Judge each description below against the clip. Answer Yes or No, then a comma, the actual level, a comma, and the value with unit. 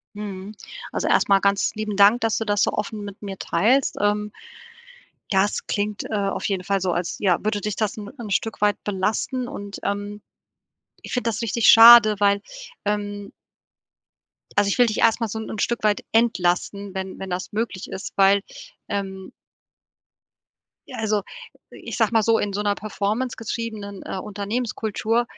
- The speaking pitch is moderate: No, high, 205 Hz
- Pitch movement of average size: No, narrow, 1.7 semitones